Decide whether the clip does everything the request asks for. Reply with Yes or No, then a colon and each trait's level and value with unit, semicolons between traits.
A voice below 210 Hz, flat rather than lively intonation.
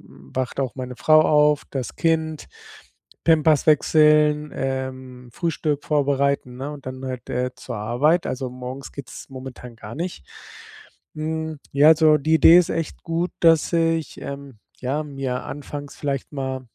No: medium, 140 Hz; average, 3.1 semitones